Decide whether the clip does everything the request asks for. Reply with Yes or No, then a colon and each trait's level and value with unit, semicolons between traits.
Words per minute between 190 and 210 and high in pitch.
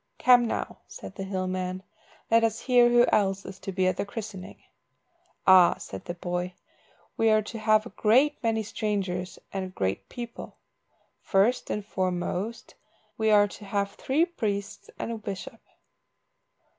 No: average, 155 wpm; high, 205 Hz